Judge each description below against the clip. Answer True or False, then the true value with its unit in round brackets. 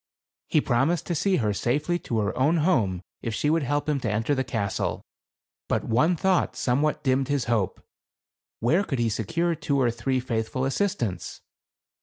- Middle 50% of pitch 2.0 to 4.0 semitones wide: False (5.3 semitones)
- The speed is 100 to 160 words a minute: False (175 wpm)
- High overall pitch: False (135 Hz)